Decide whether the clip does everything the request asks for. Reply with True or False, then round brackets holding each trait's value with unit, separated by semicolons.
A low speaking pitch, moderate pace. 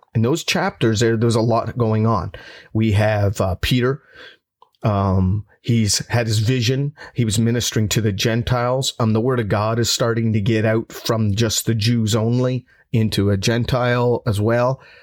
True (115 Hz; 175 wpm)